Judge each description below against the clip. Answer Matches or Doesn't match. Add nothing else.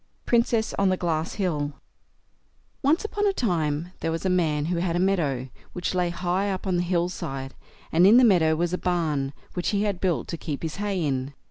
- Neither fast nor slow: Doesn't match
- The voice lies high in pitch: Doesn't match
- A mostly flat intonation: Doesn't match